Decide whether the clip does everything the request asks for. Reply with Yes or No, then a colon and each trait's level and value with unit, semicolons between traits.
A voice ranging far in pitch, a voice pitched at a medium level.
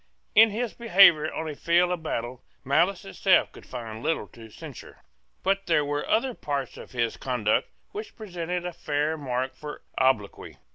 Yes: wide, 5.8 semitones; medium, 155 Hz